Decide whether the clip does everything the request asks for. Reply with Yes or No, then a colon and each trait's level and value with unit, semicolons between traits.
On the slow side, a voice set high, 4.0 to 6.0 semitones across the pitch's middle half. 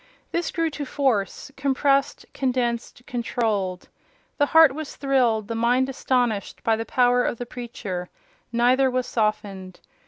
No: slow, 130 wpm; high, 245 Hz; average, 3.3 semitones